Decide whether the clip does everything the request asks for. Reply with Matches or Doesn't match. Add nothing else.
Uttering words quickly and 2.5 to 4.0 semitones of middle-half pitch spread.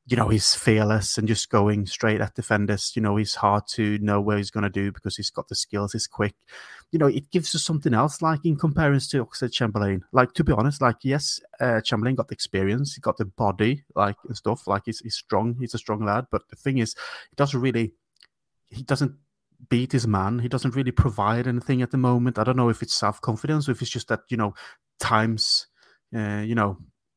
Matches